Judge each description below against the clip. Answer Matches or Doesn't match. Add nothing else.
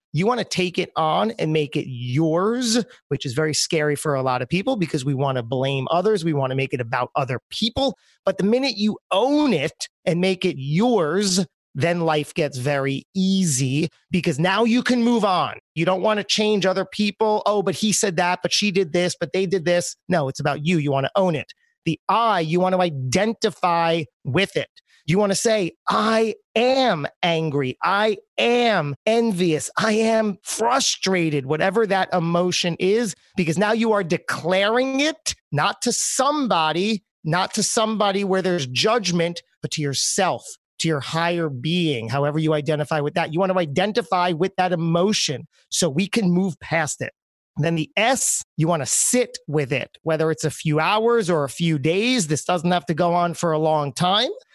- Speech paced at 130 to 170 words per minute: Doesn't match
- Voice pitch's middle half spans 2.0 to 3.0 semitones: Doesn't match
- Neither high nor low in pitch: Matches